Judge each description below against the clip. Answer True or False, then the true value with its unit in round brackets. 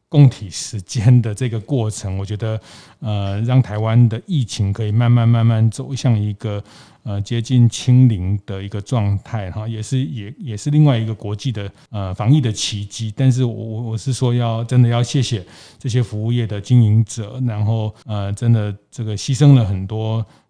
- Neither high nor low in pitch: False (115 Hz)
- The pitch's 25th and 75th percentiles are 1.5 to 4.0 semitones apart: True (3.0 semitones)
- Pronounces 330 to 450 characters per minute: False (270 characters per minute)